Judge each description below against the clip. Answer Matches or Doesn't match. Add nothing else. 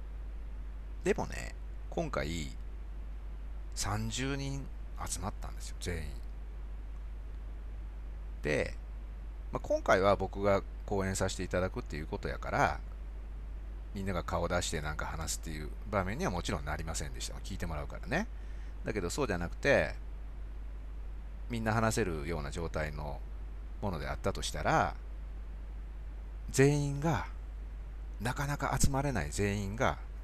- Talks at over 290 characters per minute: Doesn't match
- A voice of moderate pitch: Doesn't match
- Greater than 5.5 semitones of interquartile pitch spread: Matches